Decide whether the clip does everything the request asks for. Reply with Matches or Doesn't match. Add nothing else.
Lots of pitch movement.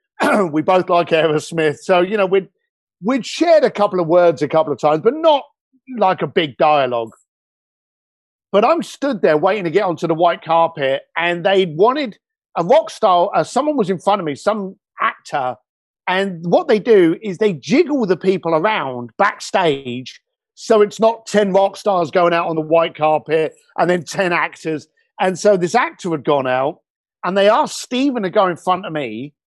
Matches